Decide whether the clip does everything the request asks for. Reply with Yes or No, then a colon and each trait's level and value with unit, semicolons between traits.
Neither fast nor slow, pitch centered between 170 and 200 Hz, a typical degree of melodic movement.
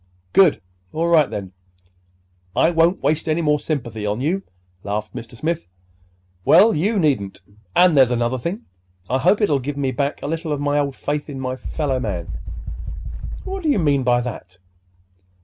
No: average, 165 wpm; medium, 145 Hz; average, 5.0 semitones